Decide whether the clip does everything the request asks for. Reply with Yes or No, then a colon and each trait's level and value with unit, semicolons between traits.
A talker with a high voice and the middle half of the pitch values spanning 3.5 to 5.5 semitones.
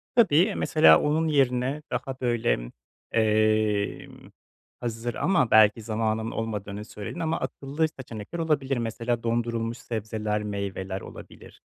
No: low, 115 Hz; average, 4.0 semitones